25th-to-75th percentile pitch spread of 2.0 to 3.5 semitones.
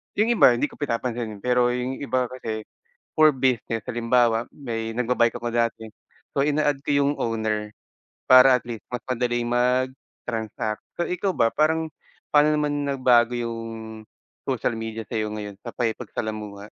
Yes: average, 2.8 semitones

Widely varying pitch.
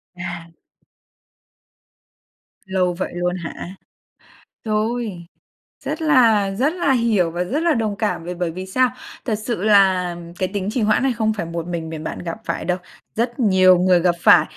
No: average, 4.4 semitones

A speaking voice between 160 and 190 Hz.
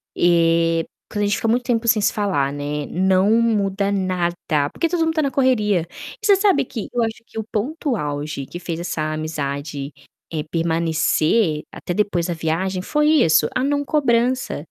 Yes: medium, 185 Hz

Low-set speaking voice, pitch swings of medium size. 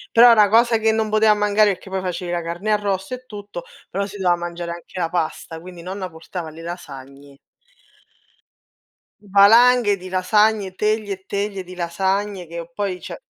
No: high, 190 Hz; average, 3.2 semitones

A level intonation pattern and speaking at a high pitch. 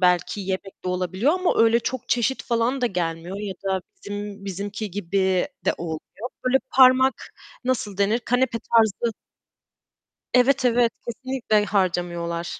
No: average, 4.6 semitones; high, 205 Hz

